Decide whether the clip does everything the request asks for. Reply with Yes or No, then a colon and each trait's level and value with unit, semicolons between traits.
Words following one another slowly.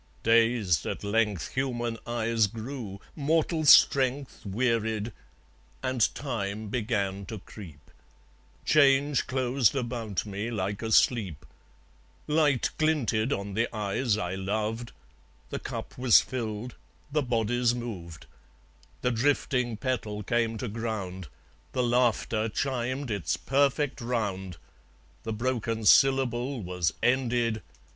Yes: slow, 110 wpm